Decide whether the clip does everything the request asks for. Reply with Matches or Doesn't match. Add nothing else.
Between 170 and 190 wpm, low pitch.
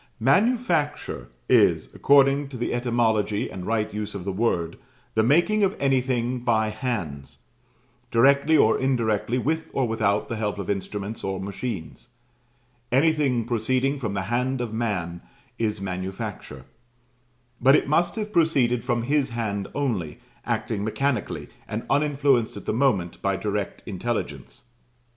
Doesn't match